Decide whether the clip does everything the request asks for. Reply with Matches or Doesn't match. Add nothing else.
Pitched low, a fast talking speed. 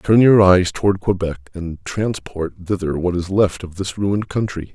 Doesn't match